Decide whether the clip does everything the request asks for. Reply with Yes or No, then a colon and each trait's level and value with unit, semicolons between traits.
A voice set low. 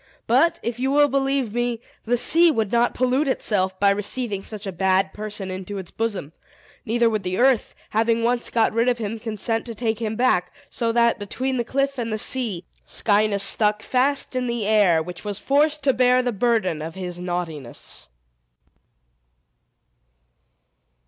No: high, 225 Hz